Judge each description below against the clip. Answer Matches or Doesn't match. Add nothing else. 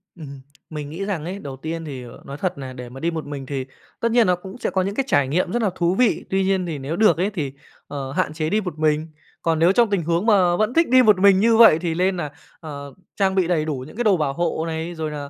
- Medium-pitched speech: Matches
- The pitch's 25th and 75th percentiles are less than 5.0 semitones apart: Matches